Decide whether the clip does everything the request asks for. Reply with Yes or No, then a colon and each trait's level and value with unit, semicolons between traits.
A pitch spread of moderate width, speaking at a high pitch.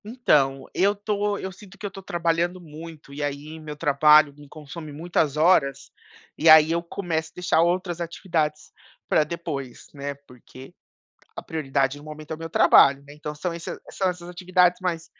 No: average, 3.1 semitones; medium, 160 Hz